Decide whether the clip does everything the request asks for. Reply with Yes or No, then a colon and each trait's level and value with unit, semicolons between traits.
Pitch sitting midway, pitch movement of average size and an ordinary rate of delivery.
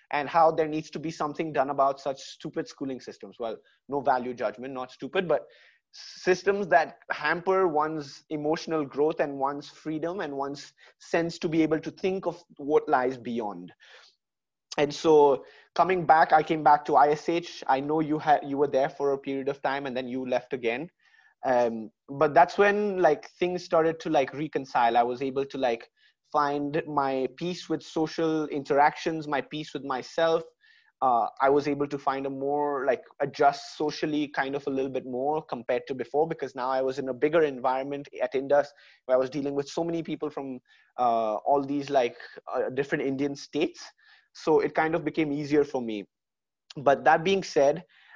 Yes: medium, 145 Hz; average, 3.0 semitones; average, 190 wpm